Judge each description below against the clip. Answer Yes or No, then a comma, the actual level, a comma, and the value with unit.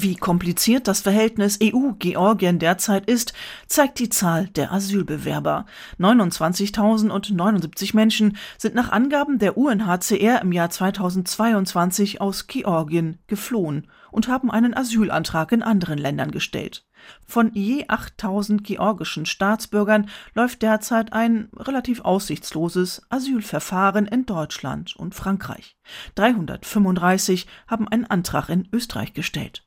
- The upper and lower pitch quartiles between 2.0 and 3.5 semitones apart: No, average, 3.9 semitones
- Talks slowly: Yes, slow, 110 wpm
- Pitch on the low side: No, high, 205 Hz